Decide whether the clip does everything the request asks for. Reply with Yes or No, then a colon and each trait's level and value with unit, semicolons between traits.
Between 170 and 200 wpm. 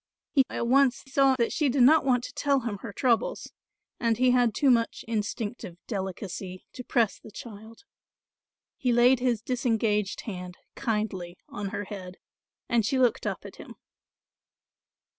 No: average, 160 wpm